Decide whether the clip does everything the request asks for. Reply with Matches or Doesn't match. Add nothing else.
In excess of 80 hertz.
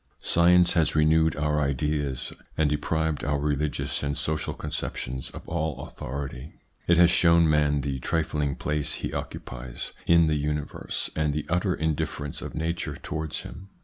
Doesn't match